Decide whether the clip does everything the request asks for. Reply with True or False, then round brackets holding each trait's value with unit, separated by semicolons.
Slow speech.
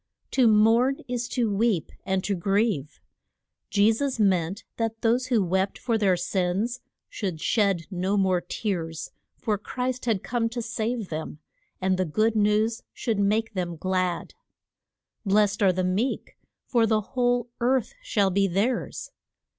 False (150 wpm)